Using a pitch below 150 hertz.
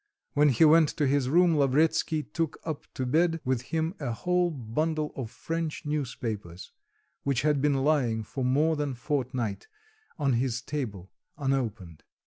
Yes: medium, 140 Hz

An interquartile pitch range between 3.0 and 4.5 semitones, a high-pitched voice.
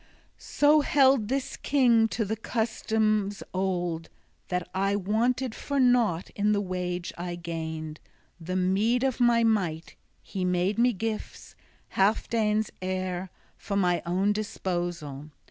Yes: average, 4.0 semitones; high, 200 Hz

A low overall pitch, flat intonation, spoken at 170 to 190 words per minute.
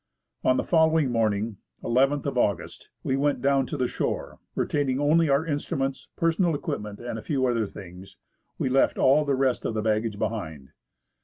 No: low, 130 Hz; average, 4.7 semitones; average, 175 wpm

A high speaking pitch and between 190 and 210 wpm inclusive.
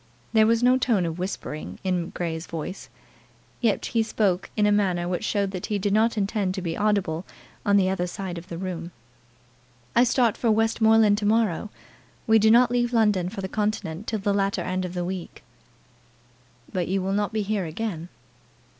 Yes: high, 200 Hz; average, 195 wpm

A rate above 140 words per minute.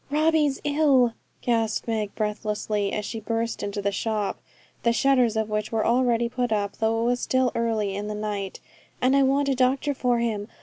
Yes: average, 200 wpm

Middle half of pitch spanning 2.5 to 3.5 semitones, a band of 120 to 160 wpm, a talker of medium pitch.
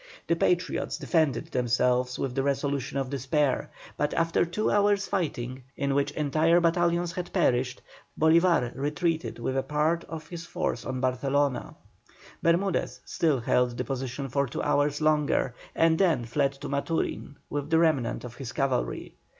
No: average, 4.2 semitones; average, 155 wpm; medium, 145 Hz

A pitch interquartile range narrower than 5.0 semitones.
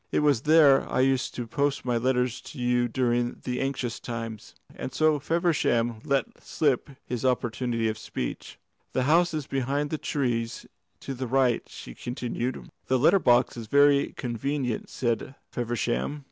Yes: average, 2.9 semitones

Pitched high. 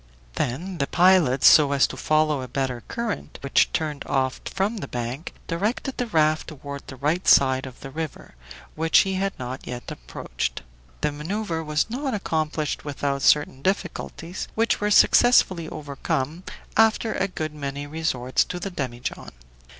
No: medium, 155 Hz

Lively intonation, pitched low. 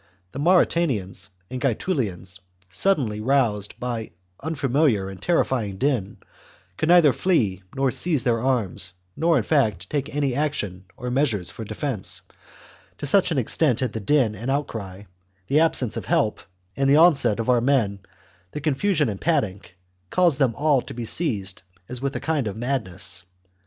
Yes: wide, 6.0 semitones; low, 130 Hz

